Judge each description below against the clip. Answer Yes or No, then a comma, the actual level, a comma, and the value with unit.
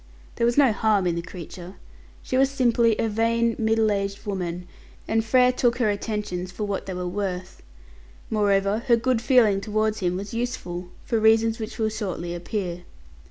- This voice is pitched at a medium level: No, high, 215 Hz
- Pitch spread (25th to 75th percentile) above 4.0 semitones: No, average, 3.5 semitones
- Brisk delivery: No, average, 175 wpm